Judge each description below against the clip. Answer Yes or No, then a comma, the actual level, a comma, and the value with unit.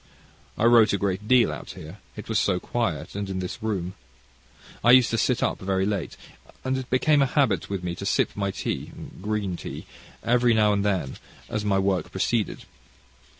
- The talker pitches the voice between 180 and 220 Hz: No, low, 105 Hz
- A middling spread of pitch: Yes, average, 3.6 semitones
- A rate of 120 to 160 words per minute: No, average, 195 wpm